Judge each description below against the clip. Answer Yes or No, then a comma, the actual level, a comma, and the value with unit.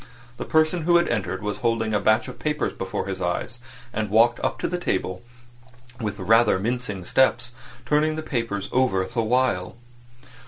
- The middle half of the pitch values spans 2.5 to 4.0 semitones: No, average, 4.7 semitones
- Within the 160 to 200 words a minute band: Yes, average, 180 wpm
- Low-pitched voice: Yes, low, 115 Hz